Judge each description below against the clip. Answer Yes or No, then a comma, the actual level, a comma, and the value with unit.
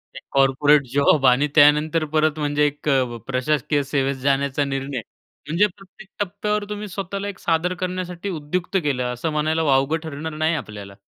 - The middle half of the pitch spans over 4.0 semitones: No, average, 3.7 semitones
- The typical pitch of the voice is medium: Yes, medium, 150 Hz